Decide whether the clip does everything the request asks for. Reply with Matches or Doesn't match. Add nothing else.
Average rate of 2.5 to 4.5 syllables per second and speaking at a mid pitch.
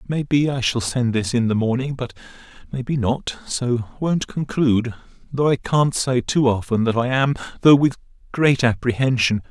Doesn't match